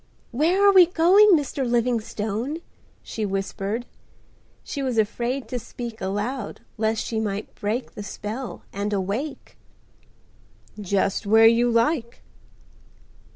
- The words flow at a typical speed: No, slow, 115 wpm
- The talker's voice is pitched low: No, high, 230 Hz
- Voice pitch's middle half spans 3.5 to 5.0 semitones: Yes, average, 4.4 semitones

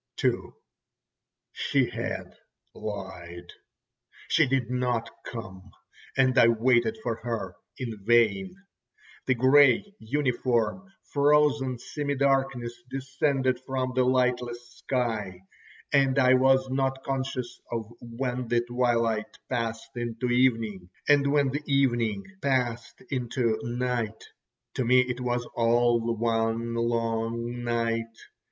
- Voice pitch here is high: No, low, 120 Hz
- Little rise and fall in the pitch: Yes, narrow, 2.3 semitones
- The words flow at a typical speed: No, slow, 110 wpm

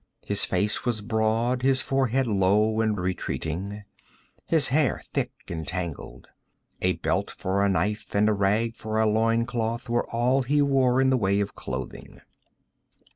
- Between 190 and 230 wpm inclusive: No, average, 160 wpm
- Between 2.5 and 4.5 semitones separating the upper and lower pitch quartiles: Yes, average, 3.7 semitones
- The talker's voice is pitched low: Yes, low, 110 Hz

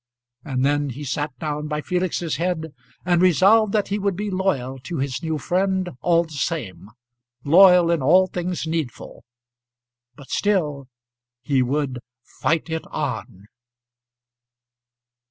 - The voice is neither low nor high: Yes, medium, 160 Hz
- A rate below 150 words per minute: Yes, slow, 135 wpm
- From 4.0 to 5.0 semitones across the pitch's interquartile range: Yes, average, 4.4 semitones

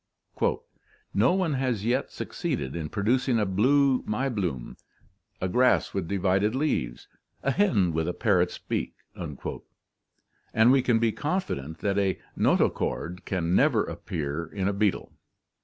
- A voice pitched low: Yes, low, 105 Hz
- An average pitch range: No, wide, 6.1 semitones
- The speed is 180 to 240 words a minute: No, average, 140 wpm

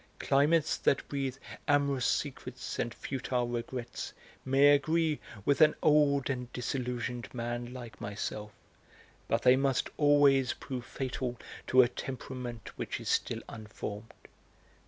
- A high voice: No, low, 130 Hz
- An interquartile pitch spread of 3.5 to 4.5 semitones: No, average, 2.7 semitones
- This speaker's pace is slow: Yes, slow, 125 wpm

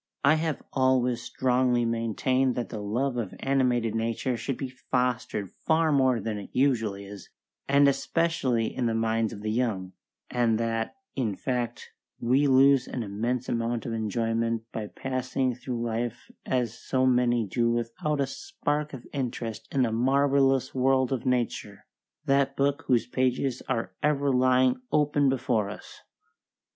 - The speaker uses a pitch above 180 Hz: No, low, 125 Hz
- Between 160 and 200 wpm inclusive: No, average, 150 wpm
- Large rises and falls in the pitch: No, average, 2.7 semitones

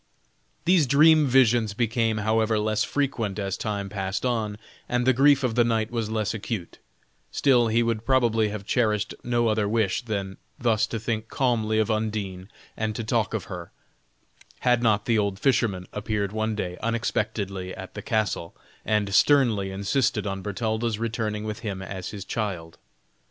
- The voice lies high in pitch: No, low, 110 Hz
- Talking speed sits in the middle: Yes, average, 165 wpm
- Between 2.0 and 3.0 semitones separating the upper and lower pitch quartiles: Yes, narrow, 2.5 semitones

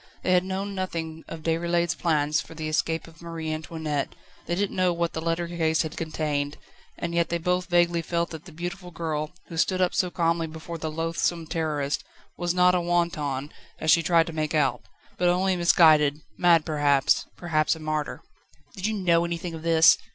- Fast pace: No, average, 195 wpm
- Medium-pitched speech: Yes, medium, 165 Hz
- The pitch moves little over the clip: Yes, narrow, 1.8 semitones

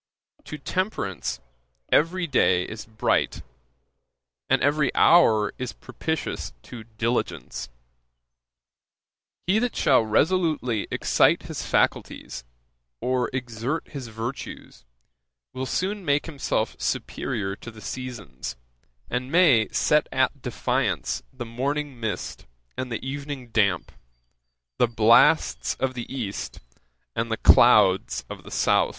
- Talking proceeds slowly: Yes, slow, 115 wpm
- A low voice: Yes, low, 125 Hz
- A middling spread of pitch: Yes, average, 4.8 semitones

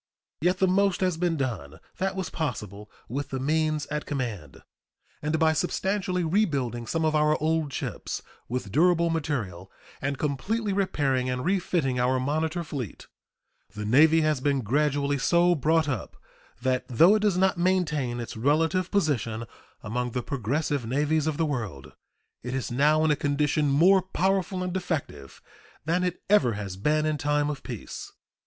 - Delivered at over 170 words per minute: No, average, 160 wpm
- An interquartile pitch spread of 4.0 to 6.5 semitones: Yes, average, 5.1 semitones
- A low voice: No, medium, 150 Hz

